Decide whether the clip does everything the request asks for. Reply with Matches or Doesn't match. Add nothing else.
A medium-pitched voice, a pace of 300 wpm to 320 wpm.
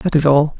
Matches